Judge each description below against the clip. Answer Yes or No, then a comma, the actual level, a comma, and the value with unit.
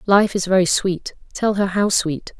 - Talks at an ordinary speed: Yes, average, 175 wpm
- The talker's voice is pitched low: No, high, 190 Hz